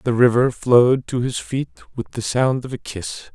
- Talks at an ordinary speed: No, fast, 215 wpm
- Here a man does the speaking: Yes, male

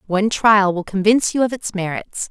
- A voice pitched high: Yes, high, 205 Hz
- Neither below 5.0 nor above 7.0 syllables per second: Yes, 5.6 syllables/s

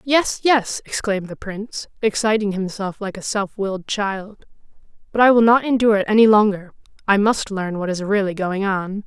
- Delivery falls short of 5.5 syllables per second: Yes, 5.2 syllables/s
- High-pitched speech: Yes, high, 205 Hz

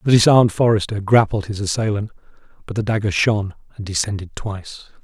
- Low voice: Yes, low, 105 Hz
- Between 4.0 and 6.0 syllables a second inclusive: No, 6.3 syllables/s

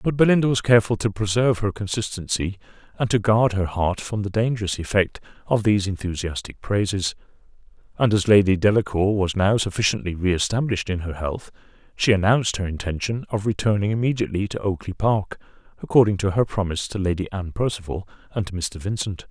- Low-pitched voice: Yes, low, 100 Hz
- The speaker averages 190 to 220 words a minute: No, average, 170 wpm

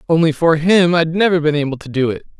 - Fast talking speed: Yes, fast, 250 wpm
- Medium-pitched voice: Yes, medium, 160 Hz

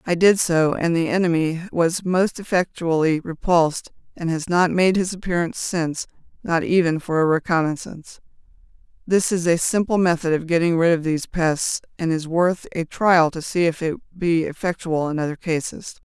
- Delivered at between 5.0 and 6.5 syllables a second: Yes, 5.1 syllables/s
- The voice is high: No, medium, 170 Hz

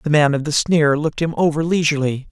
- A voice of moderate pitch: Yes, medium, 150 Hz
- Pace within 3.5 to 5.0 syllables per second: No, 6.4 syllables/s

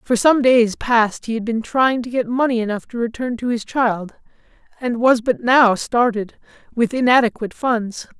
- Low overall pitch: No, high, 235 Hz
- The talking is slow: No, average, 185 wpm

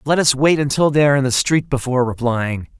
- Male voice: Yes, male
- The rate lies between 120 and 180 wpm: No, fast, 235 wpm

